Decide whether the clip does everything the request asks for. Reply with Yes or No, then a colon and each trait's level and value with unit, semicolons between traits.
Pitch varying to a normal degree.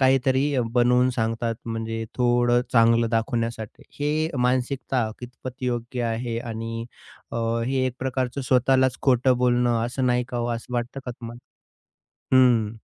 No: narrow, 1.8 semitones